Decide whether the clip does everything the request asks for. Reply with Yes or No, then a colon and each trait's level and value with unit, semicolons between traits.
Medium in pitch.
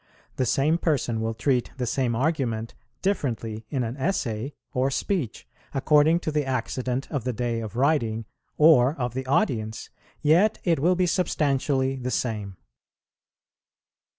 No: low, 130 Hz